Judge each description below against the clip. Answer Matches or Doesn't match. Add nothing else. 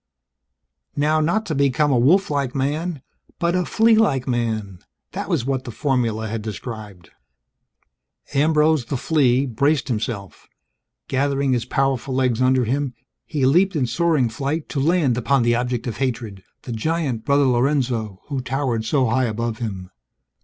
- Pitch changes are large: Doesn't match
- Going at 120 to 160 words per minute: Matches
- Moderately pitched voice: Doesn't match